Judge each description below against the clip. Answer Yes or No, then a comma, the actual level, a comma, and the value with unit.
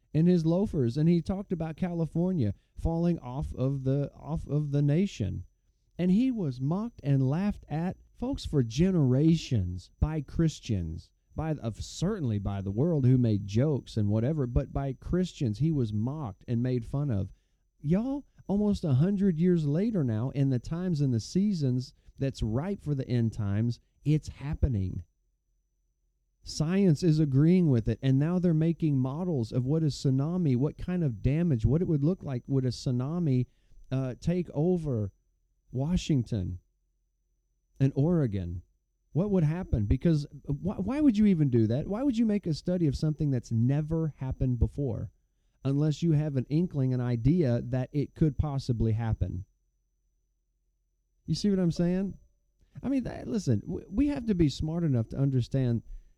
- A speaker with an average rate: Yes, average, 165 wpm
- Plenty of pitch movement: Yes, wide, 6.3 semitones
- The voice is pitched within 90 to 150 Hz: Yes, medium, 140 Hz